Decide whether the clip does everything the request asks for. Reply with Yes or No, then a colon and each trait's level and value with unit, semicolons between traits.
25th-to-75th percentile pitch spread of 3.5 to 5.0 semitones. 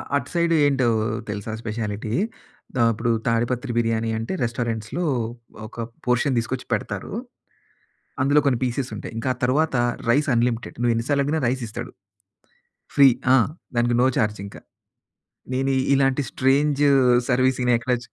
No: average, 2.9 semitones